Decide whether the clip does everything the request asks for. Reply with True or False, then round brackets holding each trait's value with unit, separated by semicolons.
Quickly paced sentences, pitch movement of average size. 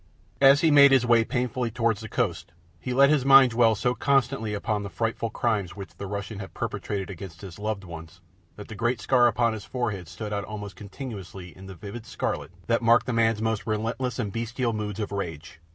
True (210 wpm; 3.3 semitones)